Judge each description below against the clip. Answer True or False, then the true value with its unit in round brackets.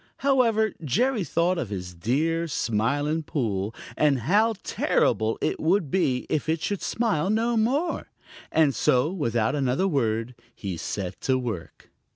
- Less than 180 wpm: True (145 wpm)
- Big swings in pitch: True (8.9 semitones)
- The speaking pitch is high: False (150 Hz)